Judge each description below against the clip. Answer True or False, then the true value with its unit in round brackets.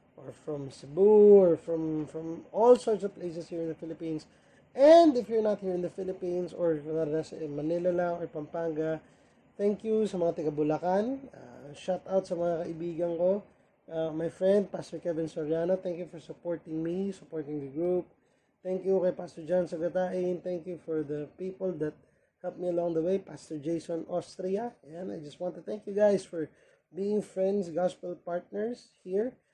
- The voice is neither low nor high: True (175 Hz)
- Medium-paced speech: True (175 wpm)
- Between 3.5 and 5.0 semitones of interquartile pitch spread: False (2.7 semitones)